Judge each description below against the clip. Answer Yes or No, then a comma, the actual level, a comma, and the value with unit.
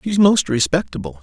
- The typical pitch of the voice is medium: Yes, medium, 145 Hz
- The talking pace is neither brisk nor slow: Yes, average, 195 wpm